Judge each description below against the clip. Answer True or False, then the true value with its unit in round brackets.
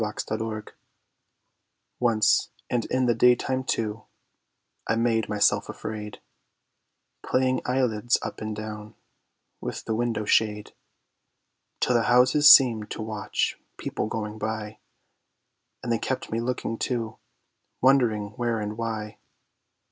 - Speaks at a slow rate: True (120 wpm)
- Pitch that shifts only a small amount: True (2.3 semitones)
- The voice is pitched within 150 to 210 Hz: False (110 Hz)